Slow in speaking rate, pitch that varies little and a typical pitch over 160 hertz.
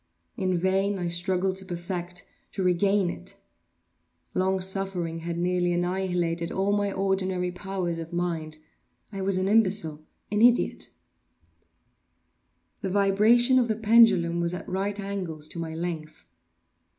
Yes: slow, 125 wpm; narrow, 2.3 semitones; medium, 185 Hz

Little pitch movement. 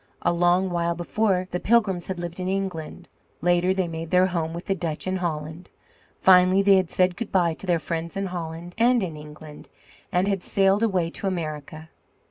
Yes: narrow, 2.3 semitones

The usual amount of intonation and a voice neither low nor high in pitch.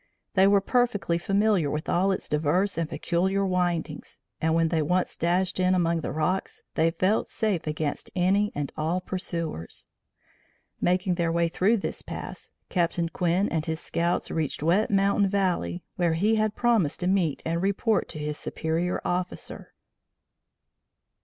Yes: average, 3.1 semitones; medium, 180 Hz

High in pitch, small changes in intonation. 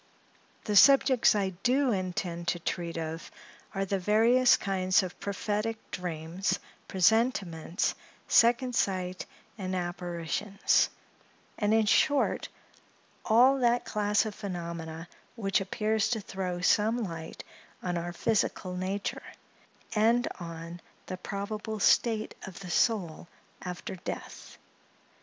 No: high, 195 Hz; average, 3.8 semitones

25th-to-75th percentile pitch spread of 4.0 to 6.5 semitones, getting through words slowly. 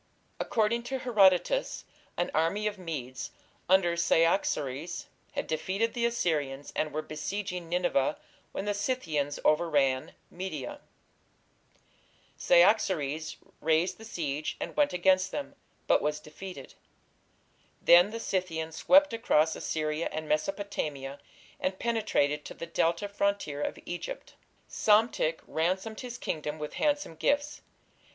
Yes: average, 5.3 semitones; slow, 120 wpm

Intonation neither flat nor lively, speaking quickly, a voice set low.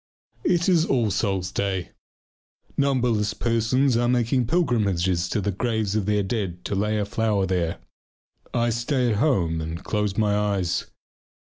No: average, 3.9 semitones; average, 150 wpm; low, 105 Hz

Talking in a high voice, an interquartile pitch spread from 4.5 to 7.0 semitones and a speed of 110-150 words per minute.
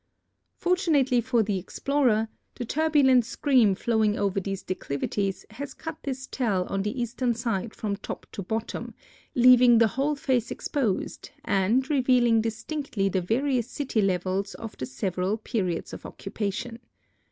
Yes: high, 230 Hz; average, 4.8 semitones; average, 140 wpm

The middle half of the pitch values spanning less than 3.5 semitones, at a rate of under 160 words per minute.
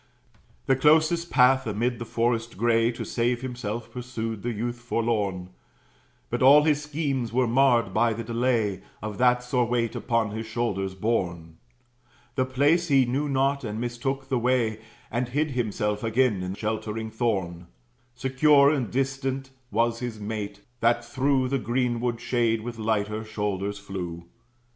Yes: average, 3.1 semitones; average, 150 wpm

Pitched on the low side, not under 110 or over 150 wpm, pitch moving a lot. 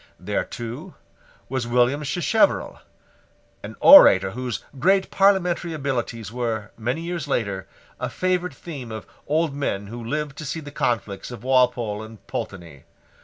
Yes: low, 125 Hz; average, 140 wpm; wide, 5.9 semitones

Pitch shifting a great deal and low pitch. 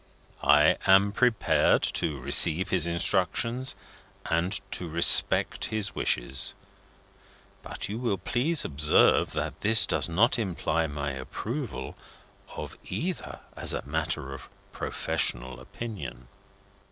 Yes: wide, 7.0 semitones; very low, 90 Hz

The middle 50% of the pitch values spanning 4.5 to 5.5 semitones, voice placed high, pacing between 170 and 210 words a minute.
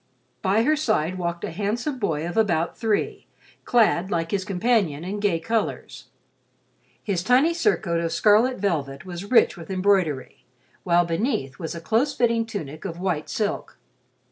No: average, 4.9 semitones; high, 195 Hz; average, 155 wpm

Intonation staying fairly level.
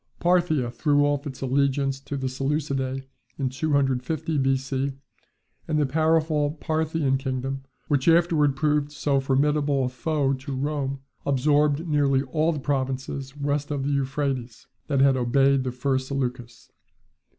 Yes: narrow, 1.9 semitones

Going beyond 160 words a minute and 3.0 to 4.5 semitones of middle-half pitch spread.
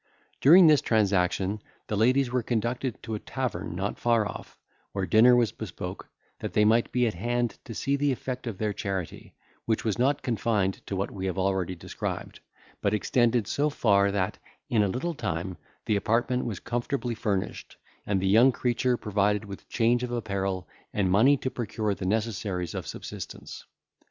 Yes: average, 175 wpm; average, 3.8 semitones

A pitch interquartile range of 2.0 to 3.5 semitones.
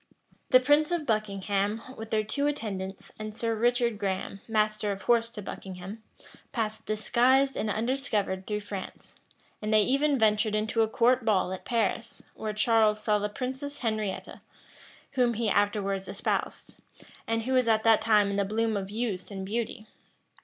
Yes: narrow, 2.5 semitones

